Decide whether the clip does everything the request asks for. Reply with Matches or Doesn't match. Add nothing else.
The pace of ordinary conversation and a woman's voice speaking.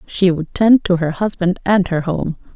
Doesn't match